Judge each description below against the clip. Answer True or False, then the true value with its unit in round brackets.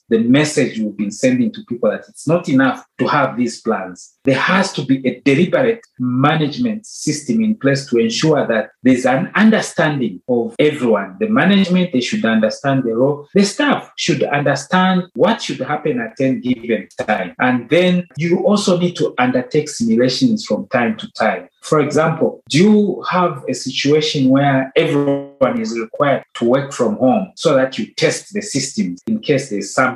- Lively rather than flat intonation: True (6.9 semitones)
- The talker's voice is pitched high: False (145 Hz)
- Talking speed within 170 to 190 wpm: True (180 wpm)